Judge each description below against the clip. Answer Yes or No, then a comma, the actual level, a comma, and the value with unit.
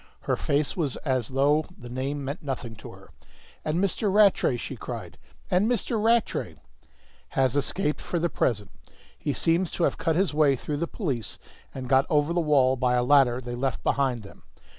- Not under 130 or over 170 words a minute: No, average, 190 wpm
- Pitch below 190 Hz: Yes, medium, 140 Hz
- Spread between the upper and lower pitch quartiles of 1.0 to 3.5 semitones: No, average, 4.7 semitones